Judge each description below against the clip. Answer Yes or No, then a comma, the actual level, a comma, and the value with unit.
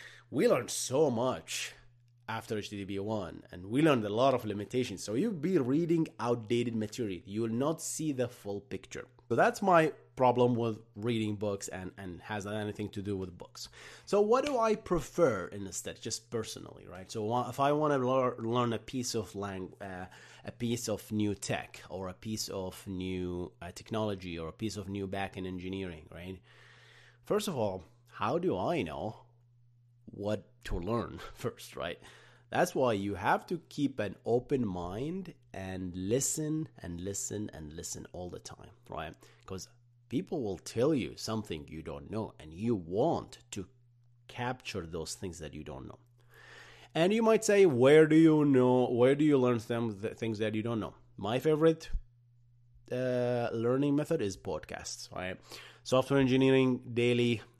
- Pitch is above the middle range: No, low, 115 Hz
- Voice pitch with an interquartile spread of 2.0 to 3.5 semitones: No, average, 4.2 semitones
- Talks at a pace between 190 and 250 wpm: No, average, 170 wpm